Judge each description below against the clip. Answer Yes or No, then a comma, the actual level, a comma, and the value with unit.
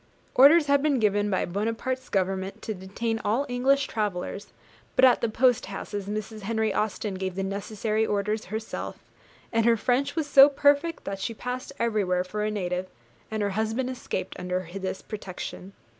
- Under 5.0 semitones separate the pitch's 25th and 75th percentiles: Yes, average, 4.1 semitones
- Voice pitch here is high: Yes, high, 215 Hz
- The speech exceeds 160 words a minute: Yes, average, 170 wpm